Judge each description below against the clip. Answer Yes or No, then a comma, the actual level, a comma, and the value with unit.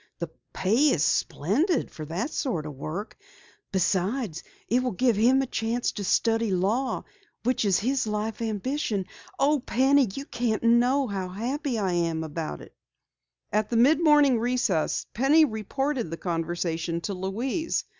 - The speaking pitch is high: Yes, high, 225 Hz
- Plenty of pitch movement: Yes, wide, 5.9 semitones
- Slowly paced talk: No, average, 155 wpm